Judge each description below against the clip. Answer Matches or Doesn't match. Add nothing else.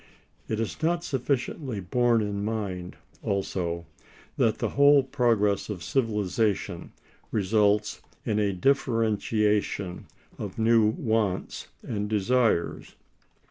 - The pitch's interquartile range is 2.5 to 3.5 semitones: Matches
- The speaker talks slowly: Matches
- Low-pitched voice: Matches